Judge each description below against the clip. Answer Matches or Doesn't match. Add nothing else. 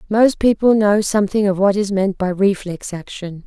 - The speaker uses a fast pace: Doesn't match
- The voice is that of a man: Doesn't match